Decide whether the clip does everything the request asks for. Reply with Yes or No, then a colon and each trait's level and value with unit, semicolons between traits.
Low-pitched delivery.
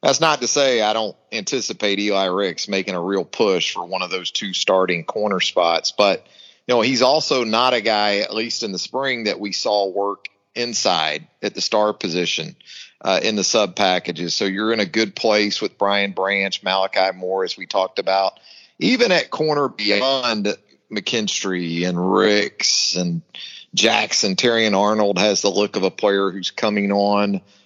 Yes: low, 100 Hz